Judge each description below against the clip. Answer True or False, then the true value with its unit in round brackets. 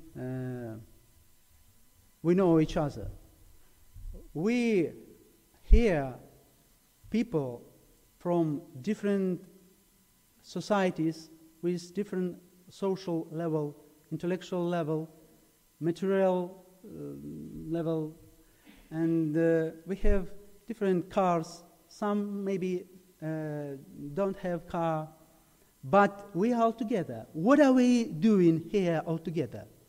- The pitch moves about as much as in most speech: True (3.5 semitones)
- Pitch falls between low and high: True (170 Hz)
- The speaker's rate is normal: False (90 wpm)